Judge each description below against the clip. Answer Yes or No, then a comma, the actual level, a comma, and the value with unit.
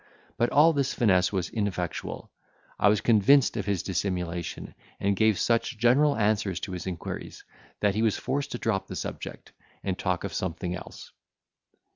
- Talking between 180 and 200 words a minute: No, average, 165 wpm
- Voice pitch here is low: Yes, low, 100 Hz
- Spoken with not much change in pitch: No, average, 4.1 semitones